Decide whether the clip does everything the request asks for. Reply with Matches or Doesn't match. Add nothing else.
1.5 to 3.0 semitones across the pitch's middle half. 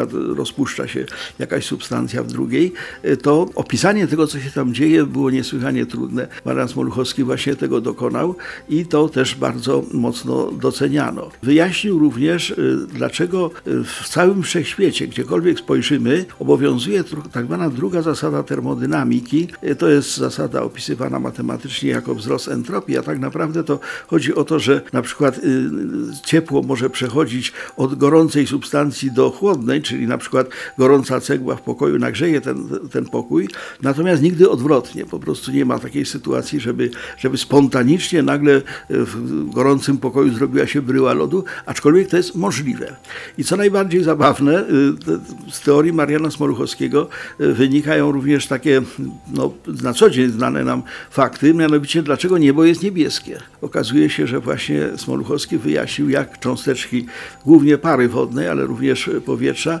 Doesn't match